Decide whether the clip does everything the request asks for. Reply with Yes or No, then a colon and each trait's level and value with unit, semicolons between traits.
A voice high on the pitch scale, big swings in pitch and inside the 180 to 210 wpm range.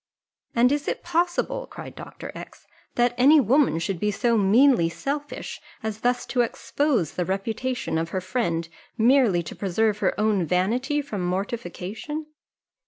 No: high, 225 Hz; wide, 6.3 semitones; average, 150 wpm